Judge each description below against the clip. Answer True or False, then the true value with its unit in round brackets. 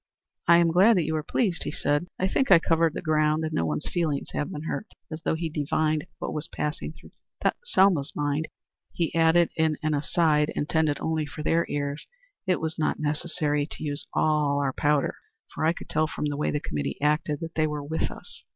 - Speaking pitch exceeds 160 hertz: False (155 Hz)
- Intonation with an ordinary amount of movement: False (1.8 semitones)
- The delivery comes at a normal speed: False (215 wpm)